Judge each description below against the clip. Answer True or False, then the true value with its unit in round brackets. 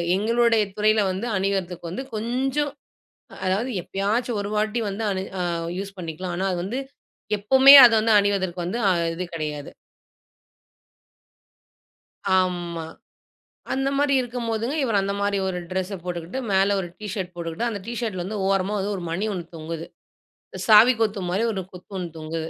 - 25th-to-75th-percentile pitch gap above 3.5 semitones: True (3.9 semitones)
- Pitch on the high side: True (200 Hz)